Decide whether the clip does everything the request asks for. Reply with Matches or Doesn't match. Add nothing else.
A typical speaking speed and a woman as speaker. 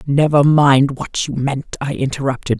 Matches